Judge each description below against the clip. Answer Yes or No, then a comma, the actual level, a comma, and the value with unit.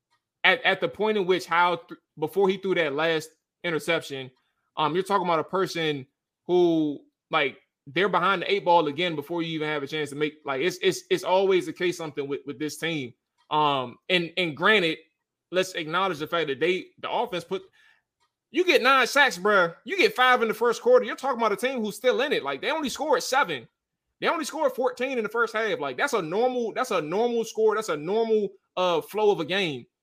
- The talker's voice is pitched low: No, high, 190 Hz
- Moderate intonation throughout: No, wide, 7.4 semitones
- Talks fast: Yes, fast, 220 wpm